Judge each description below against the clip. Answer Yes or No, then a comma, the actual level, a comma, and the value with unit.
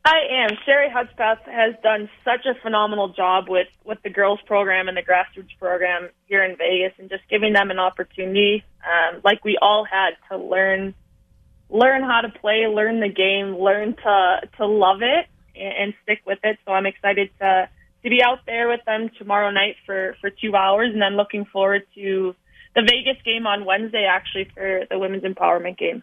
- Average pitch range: No, narrow, 2.3 semitones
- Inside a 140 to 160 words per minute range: No, average, 195 wpm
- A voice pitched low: No, high, 200 Hz